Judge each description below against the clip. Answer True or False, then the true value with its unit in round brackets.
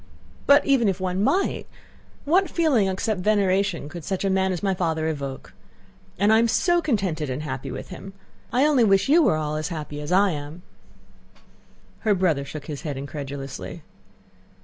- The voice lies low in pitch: False (185 Hz)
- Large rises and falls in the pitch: True (6.0 semitones)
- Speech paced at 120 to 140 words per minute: False (175 wpm)